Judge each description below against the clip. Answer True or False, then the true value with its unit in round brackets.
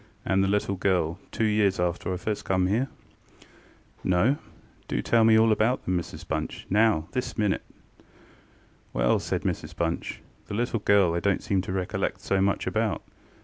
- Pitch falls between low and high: False (95 Hz)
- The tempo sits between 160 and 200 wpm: True (165 wpm)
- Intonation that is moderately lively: True (3.4 semitones)